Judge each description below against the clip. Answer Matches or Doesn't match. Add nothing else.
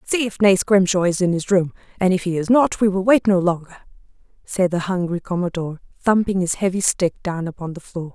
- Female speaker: Matches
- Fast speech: Matches